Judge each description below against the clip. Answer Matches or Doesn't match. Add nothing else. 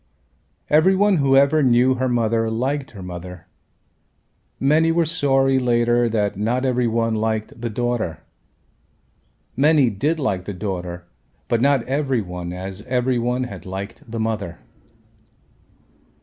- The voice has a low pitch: Matches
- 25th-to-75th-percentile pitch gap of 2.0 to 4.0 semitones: Doesn't match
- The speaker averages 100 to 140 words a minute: Matches